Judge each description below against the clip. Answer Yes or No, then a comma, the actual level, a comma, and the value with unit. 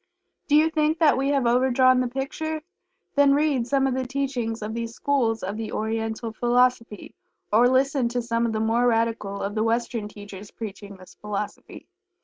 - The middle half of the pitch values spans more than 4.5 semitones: No, average, 3.3 semitones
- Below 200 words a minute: Yes, average, 180 wpm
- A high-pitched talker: Yes, high, 240 Hz